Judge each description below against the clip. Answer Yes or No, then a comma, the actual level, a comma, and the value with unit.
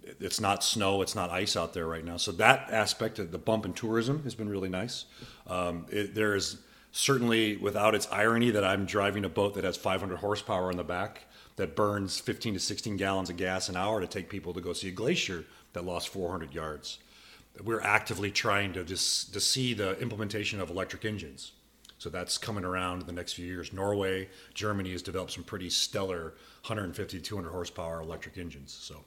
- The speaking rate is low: No, fast, 205 wpm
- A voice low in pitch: Yes, low, 100 Hz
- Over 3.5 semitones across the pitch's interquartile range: No, average, 2.8 semitones